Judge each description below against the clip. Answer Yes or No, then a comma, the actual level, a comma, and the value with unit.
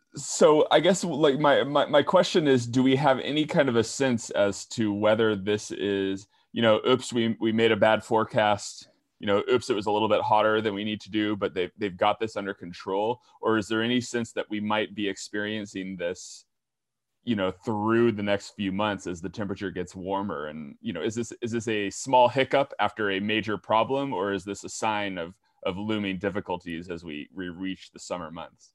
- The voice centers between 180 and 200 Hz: No, low, 105 Hz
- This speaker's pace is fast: Yes, fast, 220 wpm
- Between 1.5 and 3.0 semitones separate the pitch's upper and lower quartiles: Yes, narrow, 2.5 semitones